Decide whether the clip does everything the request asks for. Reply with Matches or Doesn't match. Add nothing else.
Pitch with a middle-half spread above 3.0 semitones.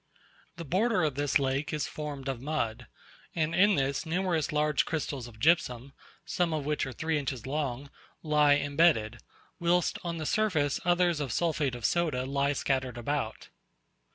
Matches